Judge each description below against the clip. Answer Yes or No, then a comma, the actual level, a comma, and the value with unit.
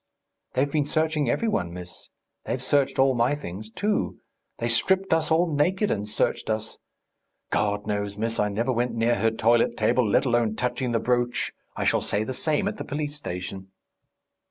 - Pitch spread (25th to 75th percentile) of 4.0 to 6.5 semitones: Yes, average, 5.1 semitones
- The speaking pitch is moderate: No, low, 120 Hz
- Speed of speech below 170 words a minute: No, average, 180 wpm